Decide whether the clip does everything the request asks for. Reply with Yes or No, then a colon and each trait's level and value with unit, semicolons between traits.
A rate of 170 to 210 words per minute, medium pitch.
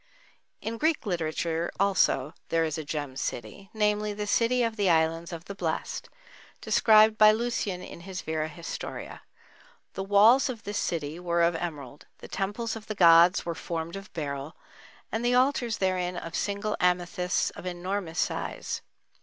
No: average, 160 wpm; medium, 180 Hz